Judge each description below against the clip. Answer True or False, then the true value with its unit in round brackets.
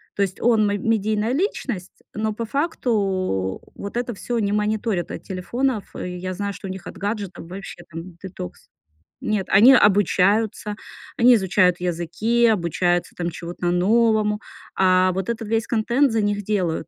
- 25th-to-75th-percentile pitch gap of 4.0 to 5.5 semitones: False (3.5 semitones)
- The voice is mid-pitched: False (205 Hz)